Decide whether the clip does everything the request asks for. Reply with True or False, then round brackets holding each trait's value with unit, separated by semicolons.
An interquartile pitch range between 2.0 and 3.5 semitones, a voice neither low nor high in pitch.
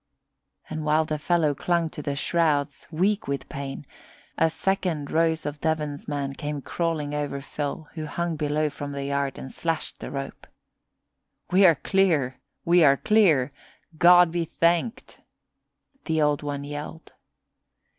True (2.7 semitones; 155 Hz)